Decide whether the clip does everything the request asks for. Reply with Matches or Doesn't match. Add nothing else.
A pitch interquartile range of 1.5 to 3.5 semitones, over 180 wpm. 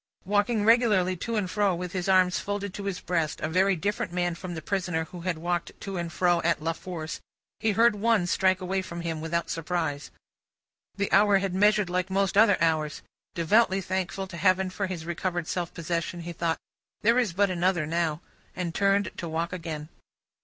Matches